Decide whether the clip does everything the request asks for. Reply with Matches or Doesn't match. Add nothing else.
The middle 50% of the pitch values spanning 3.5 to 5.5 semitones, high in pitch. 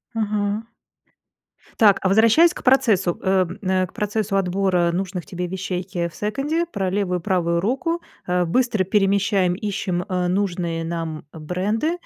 Doesn't match